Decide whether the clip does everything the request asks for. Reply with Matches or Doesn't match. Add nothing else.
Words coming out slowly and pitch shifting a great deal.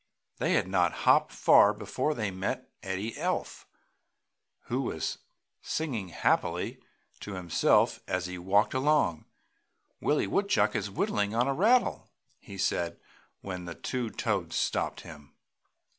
Matches